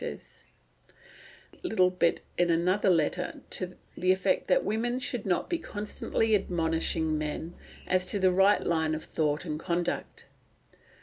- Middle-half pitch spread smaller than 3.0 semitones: No, average, 3.9 semitones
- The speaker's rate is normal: Yes, average, 160 wpm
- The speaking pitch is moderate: Yes, medium, 180 Hz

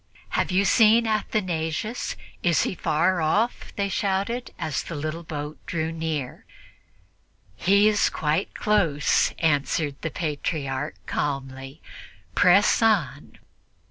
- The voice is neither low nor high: Yes, medium, 165 Hz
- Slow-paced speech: Yes, slow, 110 wpm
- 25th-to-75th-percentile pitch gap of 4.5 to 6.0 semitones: Yes, average, 5.2 semitones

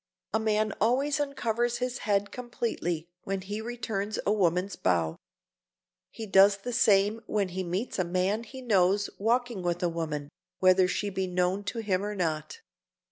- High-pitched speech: Yes, high, 200 Hz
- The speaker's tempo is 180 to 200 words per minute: No, average, 165 wpm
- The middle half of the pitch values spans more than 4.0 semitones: No, average, 3.6 semitones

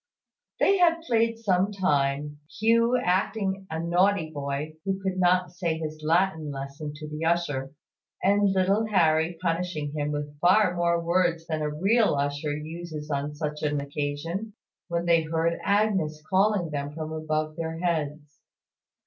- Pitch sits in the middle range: Yes, medium, 165 Hz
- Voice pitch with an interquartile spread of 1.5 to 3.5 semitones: No, average, 4.0 semitones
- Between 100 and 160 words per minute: Yes, average, 150 wpm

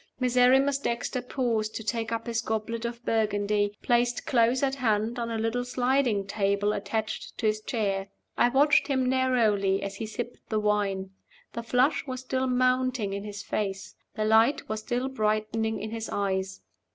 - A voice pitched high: Yes, high, 225 Hz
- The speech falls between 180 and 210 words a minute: No, average, 170 wpm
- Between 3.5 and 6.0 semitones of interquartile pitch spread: No, average, 3.1 semitones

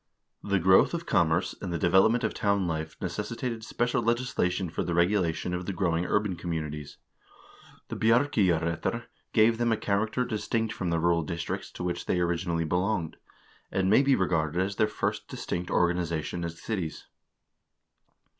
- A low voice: Yes, very low, 90 Hz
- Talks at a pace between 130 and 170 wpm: Yes, average, 160 wpm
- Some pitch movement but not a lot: Yes, average, 4.3 semitones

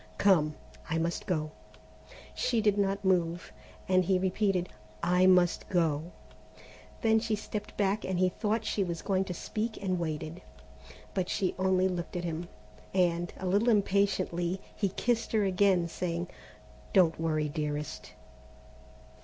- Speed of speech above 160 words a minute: No, average, 145 wpm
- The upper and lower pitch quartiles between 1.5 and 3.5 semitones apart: Yes, average, 2.8 semitones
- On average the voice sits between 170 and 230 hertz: Yes, medium, 185 Hz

